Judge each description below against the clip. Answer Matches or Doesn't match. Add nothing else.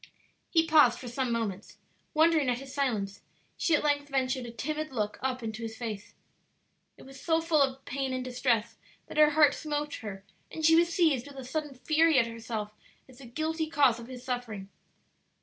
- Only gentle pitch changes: Doesn't match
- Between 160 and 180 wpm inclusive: Doesn't match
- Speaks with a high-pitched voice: Matches